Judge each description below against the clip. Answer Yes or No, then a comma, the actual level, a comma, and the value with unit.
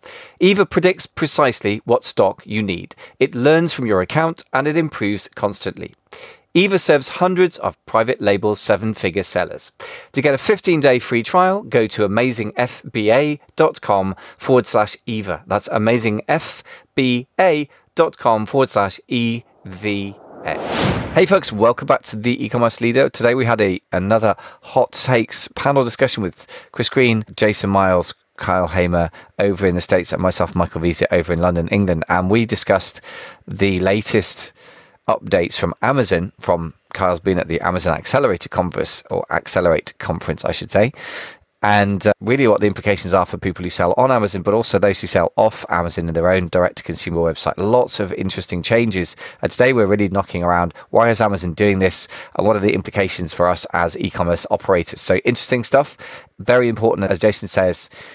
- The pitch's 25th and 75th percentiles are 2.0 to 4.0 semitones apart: No, average, 5.1 semitones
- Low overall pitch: Yes, low, 105 Hz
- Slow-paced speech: No, average, 165 wpm